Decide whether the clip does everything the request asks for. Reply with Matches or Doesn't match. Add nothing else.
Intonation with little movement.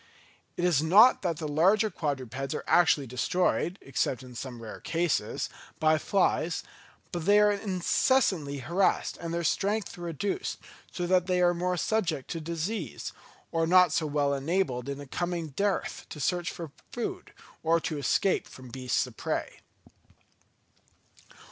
Doesn't match